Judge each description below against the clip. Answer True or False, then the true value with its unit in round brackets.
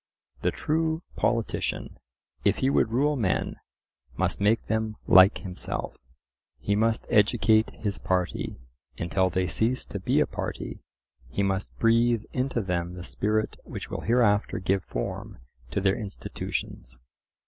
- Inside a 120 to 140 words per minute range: True (135 wpm)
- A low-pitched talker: True (105 Hz)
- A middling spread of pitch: True (3.6 semitones)